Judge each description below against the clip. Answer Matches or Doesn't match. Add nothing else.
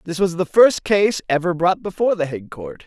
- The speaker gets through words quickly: Matches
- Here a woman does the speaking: Doesn't match